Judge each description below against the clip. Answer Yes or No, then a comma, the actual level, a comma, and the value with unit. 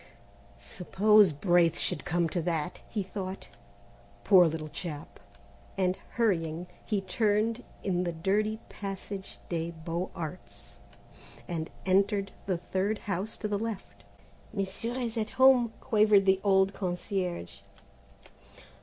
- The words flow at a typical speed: No, slow, 120 wpm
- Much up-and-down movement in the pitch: No, average, 3.3 semitones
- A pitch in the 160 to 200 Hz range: Yes, high, 190 Hz